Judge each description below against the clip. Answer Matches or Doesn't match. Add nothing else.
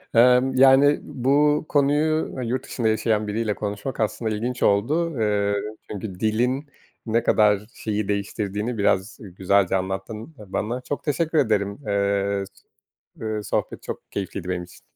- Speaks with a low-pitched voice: Matches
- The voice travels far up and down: Doesn't match